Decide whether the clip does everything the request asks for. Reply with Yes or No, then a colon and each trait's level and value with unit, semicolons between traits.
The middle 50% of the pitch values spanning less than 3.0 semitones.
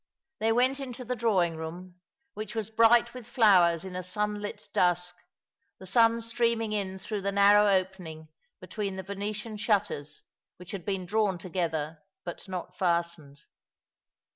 No: average, 3.8 semitones